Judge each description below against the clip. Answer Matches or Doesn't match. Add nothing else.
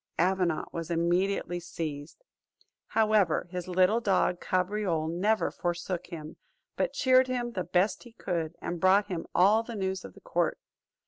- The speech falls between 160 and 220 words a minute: Doesn't match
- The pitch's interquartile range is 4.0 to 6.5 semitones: Doesn't match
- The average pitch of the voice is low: Doesn't match